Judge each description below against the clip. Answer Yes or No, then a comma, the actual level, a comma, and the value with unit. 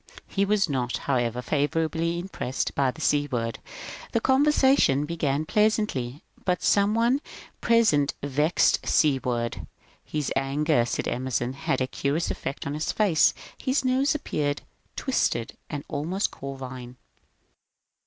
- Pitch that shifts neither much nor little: No, wide, 7.0 semitones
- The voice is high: No, medium, 150 Hz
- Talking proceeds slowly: Yes, slow, 125 wpm